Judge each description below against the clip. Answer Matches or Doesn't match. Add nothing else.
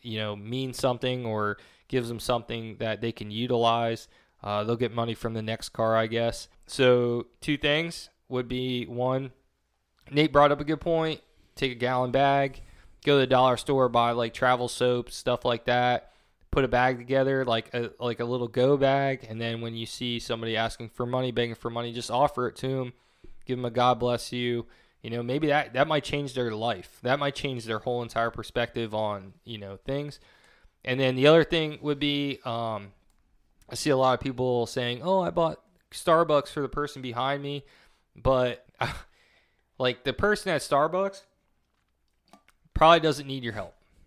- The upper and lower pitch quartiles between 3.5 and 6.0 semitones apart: Doesn't match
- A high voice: Doesn't match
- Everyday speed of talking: Matches